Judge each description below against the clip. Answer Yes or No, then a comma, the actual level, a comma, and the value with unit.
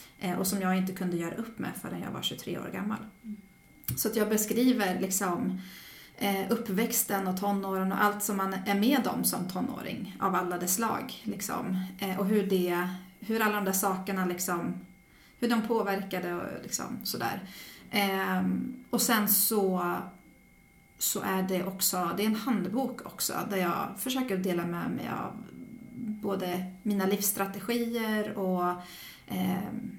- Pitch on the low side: No, high, 200 Hz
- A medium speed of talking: Yes, average, 155 wpm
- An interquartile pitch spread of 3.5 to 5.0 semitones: No, average, 2.7 semitones